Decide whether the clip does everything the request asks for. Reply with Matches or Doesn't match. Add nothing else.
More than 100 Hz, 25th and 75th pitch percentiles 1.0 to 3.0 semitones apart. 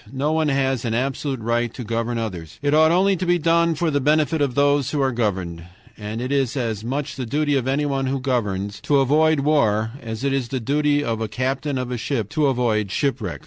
Doesn't match